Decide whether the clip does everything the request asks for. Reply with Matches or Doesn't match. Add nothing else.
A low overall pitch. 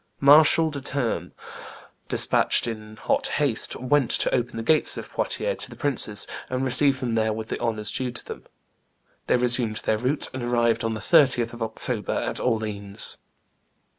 Matches